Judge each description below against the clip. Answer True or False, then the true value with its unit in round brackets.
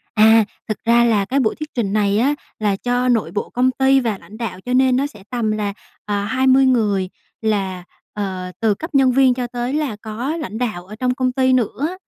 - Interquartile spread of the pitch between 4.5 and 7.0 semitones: False (3.8 semitones)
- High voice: True (235 Hz)